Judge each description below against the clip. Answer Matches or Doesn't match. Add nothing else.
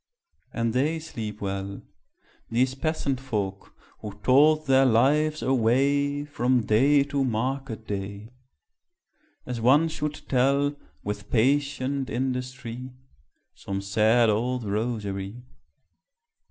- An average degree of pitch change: Matches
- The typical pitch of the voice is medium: Doesn't match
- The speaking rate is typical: Doesn't match